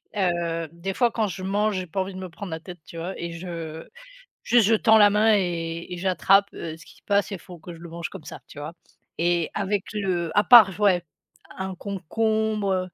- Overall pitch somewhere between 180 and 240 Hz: Yes, medium, 185 Hz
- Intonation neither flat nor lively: Yes, average, 3.1 semitones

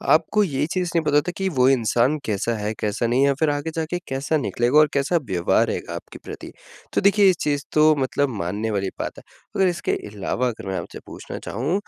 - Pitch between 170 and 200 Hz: No, medium, 140 Hz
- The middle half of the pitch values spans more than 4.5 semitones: Yes, wide, 5.5 semitones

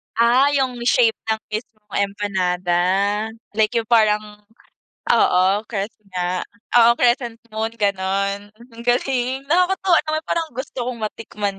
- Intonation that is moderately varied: Yes, average, 3.3 semitones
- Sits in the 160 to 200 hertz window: No, high, 220 Hz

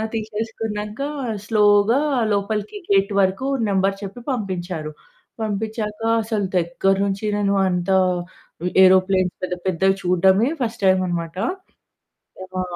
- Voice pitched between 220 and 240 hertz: No, high, 195 Hz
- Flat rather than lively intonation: Yes, narrow, 2.3 semitones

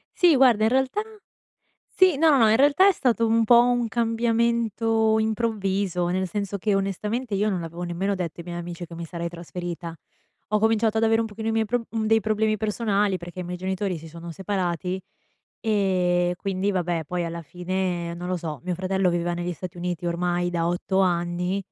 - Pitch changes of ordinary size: Yes, average, 4.0 semitones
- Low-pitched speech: No, high, 190 Hz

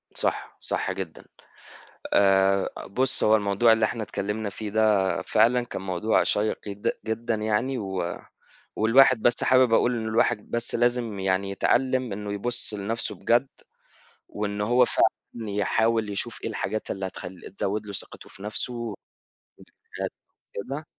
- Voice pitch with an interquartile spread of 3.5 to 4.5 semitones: No, average, 2.9 semitones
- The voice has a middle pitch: No, low, 110 Hz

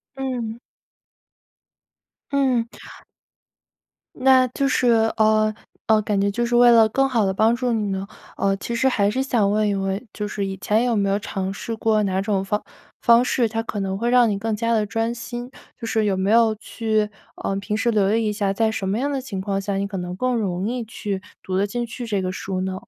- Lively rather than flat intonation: No, average, 3.1 semitones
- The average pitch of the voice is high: Yes, high, 215 Hz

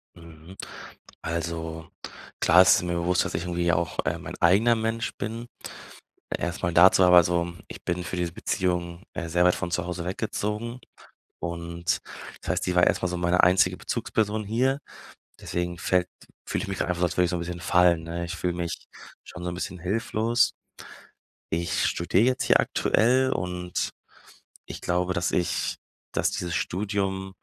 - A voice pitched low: Yes, very low, 90 Hz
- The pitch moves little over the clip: Yes, narrow, 2.0 semitones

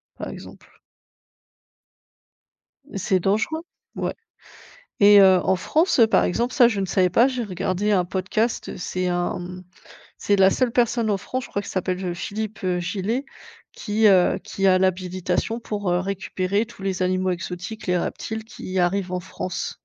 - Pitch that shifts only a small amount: No, average, 3.0 semitones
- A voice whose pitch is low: No, high, 195 Hz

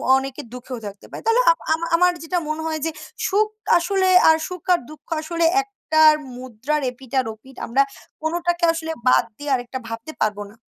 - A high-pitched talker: Yes, very high, 310 Hz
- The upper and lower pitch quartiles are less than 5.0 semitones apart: No, wide, 5.4 semitones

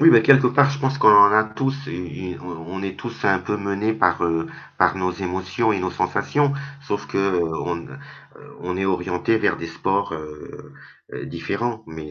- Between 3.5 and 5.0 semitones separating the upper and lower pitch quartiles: Yes, average, 4.0 semitones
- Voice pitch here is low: Yes, very low, 95 Hz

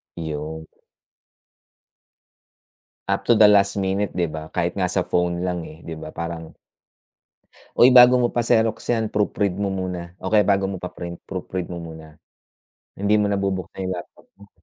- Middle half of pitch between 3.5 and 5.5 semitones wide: No, average, 2.9 semitones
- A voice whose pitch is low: Yes, very low, 95 Hz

